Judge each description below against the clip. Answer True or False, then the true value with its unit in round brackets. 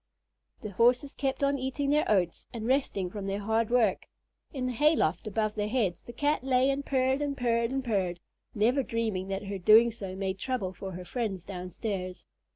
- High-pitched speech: True (225 Hz)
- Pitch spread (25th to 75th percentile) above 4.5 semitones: True (5.1 semitones)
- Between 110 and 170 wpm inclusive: False (195 wpm)